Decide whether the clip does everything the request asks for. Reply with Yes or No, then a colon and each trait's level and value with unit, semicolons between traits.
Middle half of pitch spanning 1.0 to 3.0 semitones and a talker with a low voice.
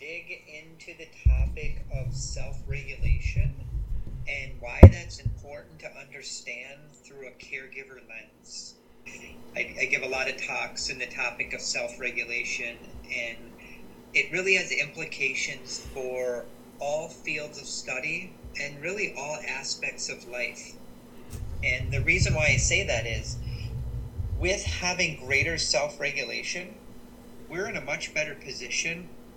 No: average, 4.9 semitones; low, 125 Hz